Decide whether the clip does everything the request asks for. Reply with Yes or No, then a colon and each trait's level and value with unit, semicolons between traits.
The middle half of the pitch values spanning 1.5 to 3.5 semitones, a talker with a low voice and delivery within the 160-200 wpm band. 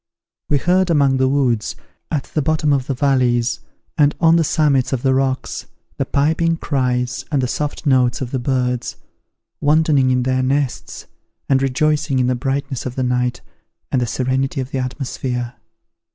Yes: narrow, 2.4 semitones; low, 130 Hz; average, 170 wpm